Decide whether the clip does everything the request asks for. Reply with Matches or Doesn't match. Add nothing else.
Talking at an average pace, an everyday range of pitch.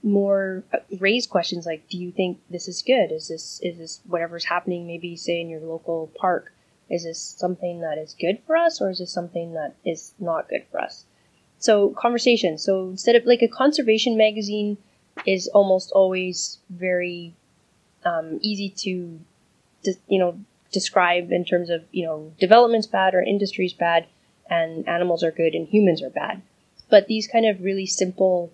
Matches